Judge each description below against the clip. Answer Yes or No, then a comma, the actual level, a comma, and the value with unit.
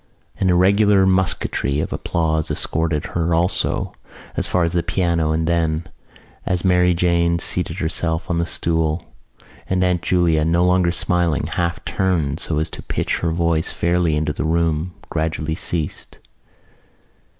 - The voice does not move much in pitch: Yes, narrow, 1.8 semitones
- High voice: No, very low, 85 Hz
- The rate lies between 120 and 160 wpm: Yes, average, 150 wpm